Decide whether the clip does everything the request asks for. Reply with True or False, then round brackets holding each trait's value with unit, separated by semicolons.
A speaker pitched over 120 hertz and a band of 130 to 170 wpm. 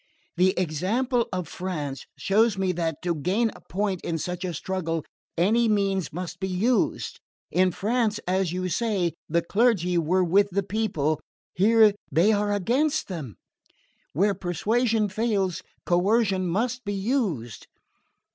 True (190 Hz; 140 wpm)